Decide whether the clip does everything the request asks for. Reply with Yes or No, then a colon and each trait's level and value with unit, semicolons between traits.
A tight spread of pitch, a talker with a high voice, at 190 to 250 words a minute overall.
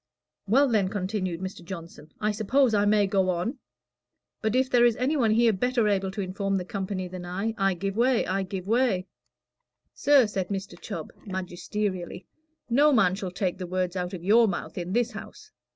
No: average, 3.6 semitones; high, 195 Hz; average, 195 wpm